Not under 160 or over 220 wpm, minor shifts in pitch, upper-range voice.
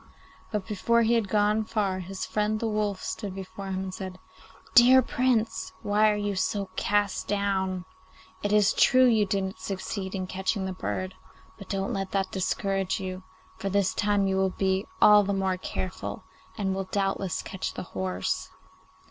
Yes: average, 175 wpm; narrow, 1.7 semitones; high, 195 Hz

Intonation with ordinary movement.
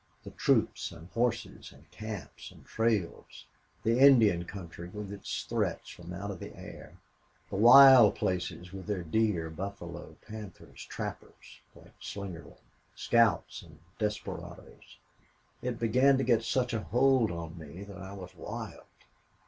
Yes: average, 4.7 semitones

